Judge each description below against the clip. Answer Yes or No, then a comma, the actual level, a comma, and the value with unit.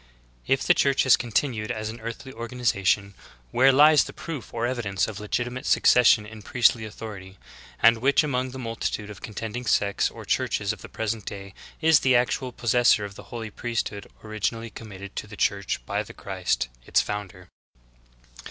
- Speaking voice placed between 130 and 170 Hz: No, low, 115 Hz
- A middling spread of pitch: Yes, average, 3.3 semitones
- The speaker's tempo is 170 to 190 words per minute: Yes, average, 180 wpm